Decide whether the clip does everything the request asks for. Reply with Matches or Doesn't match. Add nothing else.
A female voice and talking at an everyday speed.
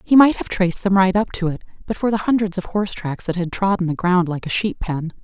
Doesn't match